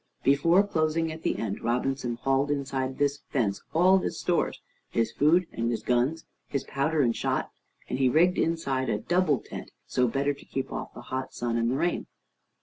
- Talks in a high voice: No, medium, 140 Hz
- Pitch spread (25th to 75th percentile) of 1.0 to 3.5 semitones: No, average, 4.2 semitones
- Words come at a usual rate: Yes, average, 190 wpm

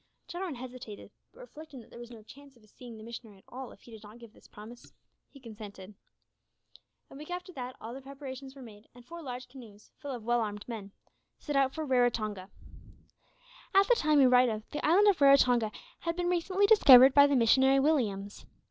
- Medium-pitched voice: No, very high, 255 Hz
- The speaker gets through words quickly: Yes, fast, 210 wpm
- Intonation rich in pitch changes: No, average, 4.2 semitones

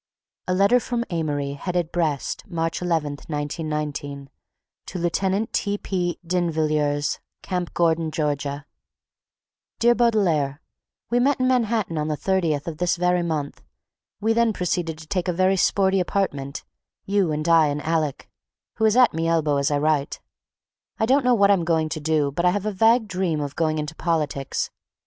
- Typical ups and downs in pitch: Yes, average, 4.3 semitones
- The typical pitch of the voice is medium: Yes, medium, 165 Hz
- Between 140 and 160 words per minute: No, average, 170 wpm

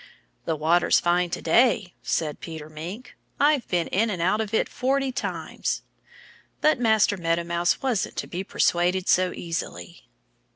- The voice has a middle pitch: Yes, medium, 180 Hz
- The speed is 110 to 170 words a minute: Yes, average, 155 wpm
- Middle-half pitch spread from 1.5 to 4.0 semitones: No, average, 4.7 semitones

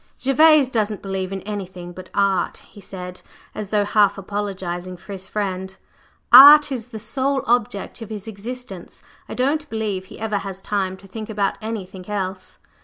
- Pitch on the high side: Yes, high, 205 Hz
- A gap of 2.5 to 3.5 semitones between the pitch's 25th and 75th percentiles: Yes, average, 3.0 semitones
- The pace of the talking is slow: No, average, 170 wpm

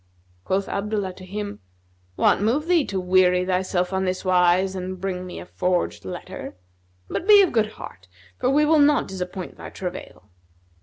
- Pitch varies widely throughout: No, average, 2.9 semitones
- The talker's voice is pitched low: No, high, 190 Hz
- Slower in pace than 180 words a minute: Yes, average, 170 wpm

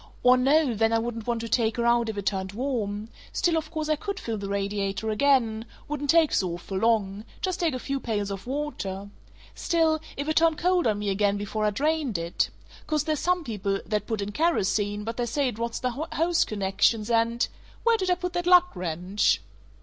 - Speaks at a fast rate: Yes, fast, 215 wpm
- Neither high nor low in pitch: No, high, 230 Hz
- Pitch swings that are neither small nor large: No, wide, 7.0 semitones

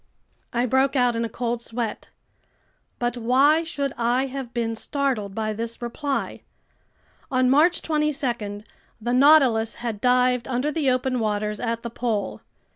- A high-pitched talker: Yes, high, 245 Hz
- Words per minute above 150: No, average, 145 wpm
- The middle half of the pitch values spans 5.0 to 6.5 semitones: No, average, 2.8 semitones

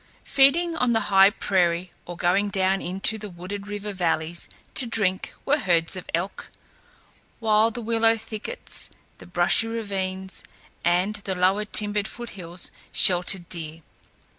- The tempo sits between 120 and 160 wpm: Yes, average, 140 wpm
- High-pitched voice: Yes, high, 195 Hz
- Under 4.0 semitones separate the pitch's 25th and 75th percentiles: Yes, average, 3.4 semitones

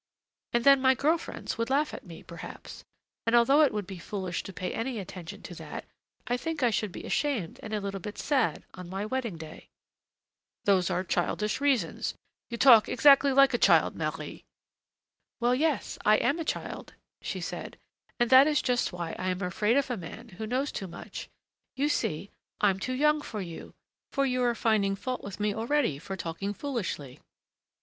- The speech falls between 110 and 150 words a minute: No, average, 190 wpm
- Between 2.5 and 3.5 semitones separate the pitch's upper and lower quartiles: No, wide, 5.6 semitones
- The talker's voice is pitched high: Yes, high, 225 Hz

